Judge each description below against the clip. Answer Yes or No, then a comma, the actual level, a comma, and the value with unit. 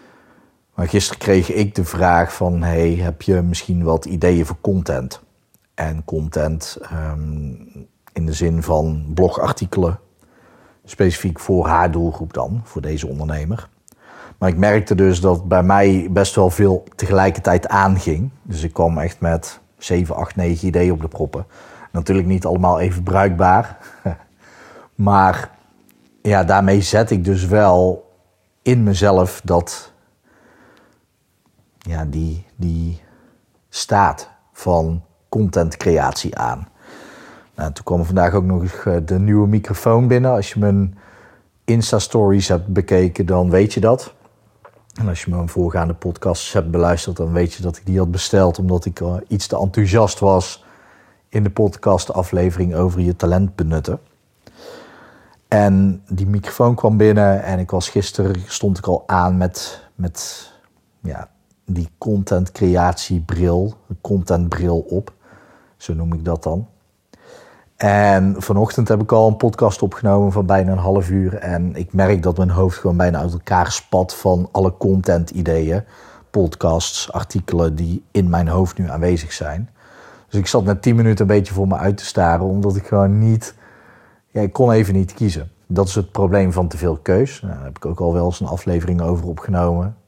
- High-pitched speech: No, very low, 95 Hz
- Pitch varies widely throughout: No, narrow, 2.4 semitones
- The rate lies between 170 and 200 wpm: No, average, 155 wpm